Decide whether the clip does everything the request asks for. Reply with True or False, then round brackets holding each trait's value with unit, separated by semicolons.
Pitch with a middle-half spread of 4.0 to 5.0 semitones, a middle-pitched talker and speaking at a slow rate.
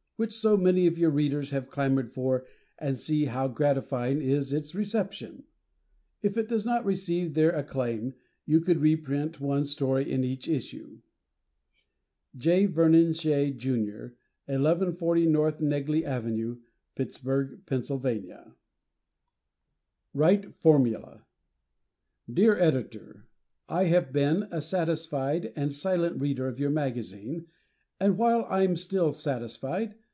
True (4.5 semitones; 145 Hz; 120 wpm)